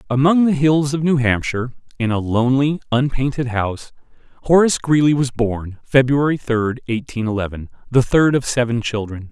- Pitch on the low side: Yes, low, 130 Hz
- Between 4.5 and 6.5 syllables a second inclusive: Yes, 5.3 syllables/s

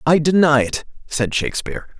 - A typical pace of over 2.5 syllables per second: Yes, 5.6 syllables/s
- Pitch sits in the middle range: Yes, medium, 150 Hz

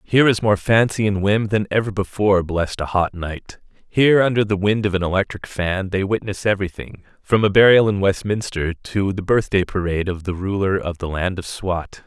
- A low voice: Yes, low, 100 Hz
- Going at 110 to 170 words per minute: No, fast, 205 wpm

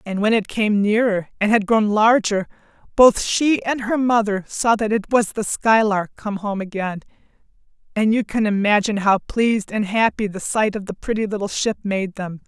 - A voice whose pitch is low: No, high, 210 Hz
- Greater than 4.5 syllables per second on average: Yes, 4.9 syllables/s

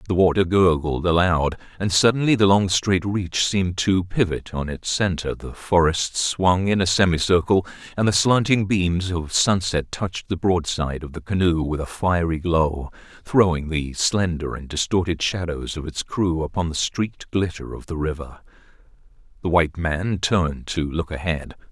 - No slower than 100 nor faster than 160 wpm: No, average, 170 wpm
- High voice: No, very low, 90 Hz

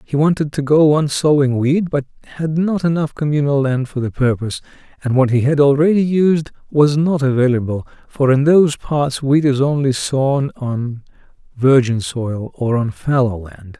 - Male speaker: Yes, male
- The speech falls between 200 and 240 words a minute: No, average, 175 wpm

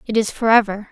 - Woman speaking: Yes, female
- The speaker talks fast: Yes, fast, 260 wpm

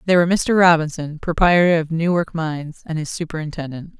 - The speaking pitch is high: No, medium, 165 Hz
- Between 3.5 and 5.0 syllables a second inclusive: No, 5.9 syllables/s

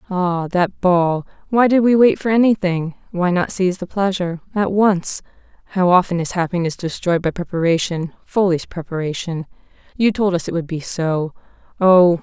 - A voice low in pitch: No, medium, 180 Hz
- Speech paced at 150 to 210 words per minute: No, average, 140 wpm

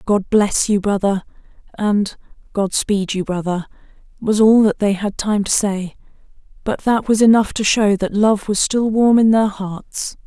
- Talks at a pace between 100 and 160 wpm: No, average, 180 wpm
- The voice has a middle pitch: No, high, 205 Hz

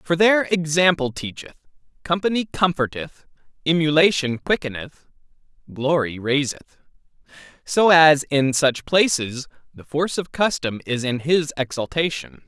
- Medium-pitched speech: Yes, medium, 150 Hz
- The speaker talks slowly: Yes, slow, 110 wpm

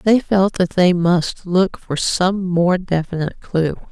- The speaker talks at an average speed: Yes, average, 170 wpm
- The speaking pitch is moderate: Yes, medium, 180 Hz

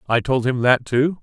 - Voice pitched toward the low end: Yes, low, 130 Hz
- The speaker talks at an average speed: No, fast, 245 wpm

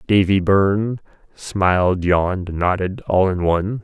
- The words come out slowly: Yes, slow, 95 wpm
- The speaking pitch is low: Yes, very low, 95 Hz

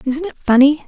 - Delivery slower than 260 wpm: Yes, fast, 205 wpm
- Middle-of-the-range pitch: No, very high, 285 Hz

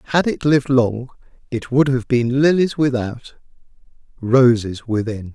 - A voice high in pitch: No, low, 125 Hz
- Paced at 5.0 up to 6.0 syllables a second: No, 4.4 syllables/s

